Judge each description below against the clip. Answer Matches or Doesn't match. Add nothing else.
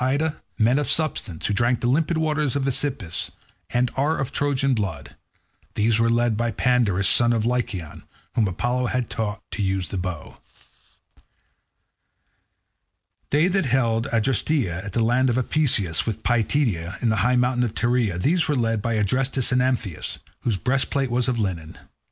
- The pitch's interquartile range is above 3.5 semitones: Matches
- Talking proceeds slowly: Doesn't match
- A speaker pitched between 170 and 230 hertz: Doesn't match